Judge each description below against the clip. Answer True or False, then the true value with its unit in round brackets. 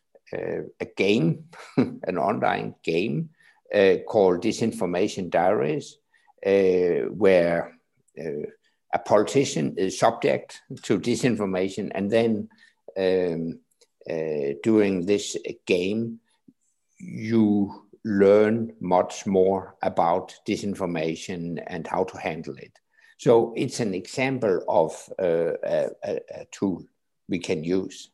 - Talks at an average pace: False (105 wpm)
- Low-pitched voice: True (115 Hz)